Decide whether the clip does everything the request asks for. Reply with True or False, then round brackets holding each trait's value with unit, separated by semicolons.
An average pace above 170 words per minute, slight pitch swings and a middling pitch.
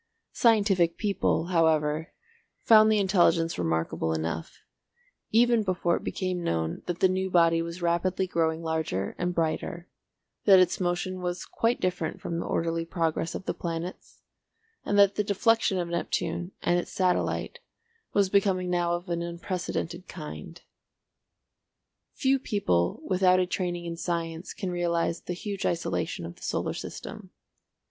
False (145 wpm; 2.2 semitones; 175 Hz)